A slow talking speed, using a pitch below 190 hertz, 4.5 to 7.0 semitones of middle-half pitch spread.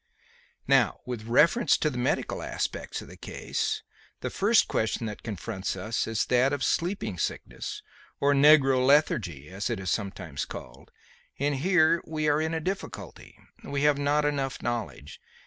No: average, 160 wpm; low, 135 Hz; wide, 5.4 semitones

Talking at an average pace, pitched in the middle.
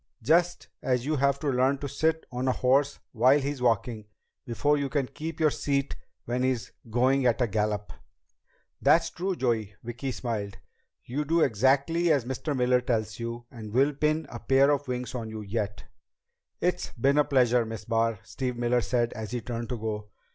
No: average, 185 wpm; low, 125 Hz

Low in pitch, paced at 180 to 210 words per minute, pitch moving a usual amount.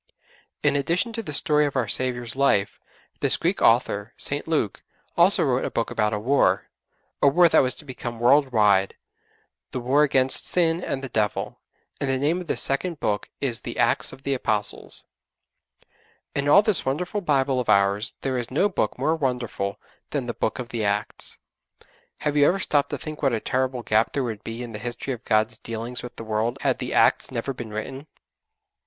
Yes: low, 130 Hz; average, 200 wpm; average, 4.2 semitones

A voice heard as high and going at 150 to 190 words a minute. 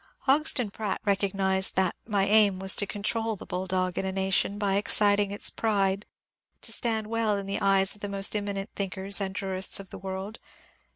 Yes: high, 200 Hz; average, 185 wpm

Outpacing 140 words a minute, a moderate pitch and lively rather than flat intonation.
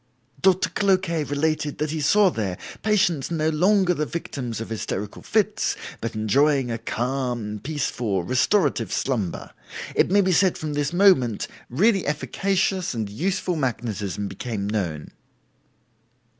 No: slow, 135 wpm; medium, 145 Hz; wide, 8.0 semitones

